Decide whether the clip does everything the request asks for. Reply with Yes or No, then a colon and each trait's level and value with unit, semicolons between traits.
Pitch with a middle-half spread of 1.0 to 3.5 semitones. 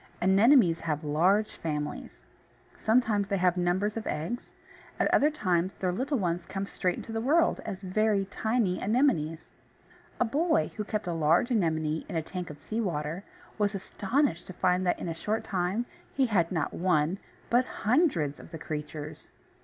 No: average, 5.0 semitones